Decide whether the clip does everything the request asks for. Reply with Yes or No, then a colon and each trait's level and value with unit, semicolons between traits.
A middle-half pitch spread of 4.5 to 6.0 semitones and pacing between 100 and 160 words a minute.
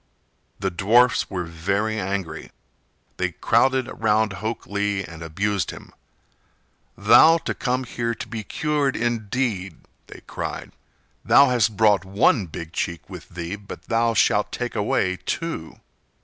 No: average, 4.0 semitones; slow, 135 wpm